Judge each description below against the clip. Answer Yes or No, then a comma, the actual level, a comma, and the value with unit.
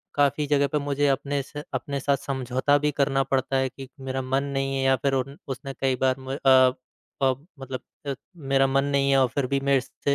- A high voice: No, low, 135 Hz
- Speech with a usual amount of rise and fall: No, narrow, 1.0 semitones